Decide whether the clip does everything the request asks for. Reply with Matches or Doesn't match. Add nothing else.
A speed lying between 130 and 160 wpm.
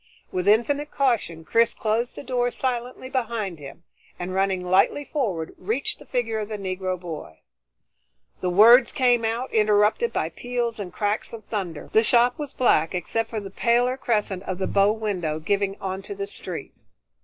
Doesn't match